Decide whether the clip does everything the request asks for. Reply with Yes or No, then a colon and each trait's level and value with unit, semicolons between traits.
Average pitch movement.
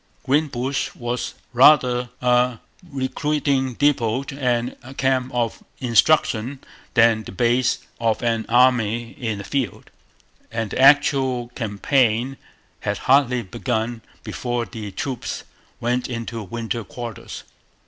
No: narrow, 2.3 semitones